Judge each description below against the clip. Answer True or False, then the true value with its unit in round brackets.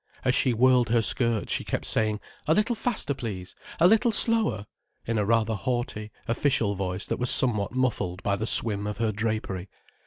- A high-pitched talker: False (115 Hz)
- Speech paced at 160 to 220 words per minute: True (175 wpm)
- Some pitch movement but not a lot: True (3.8 semitones)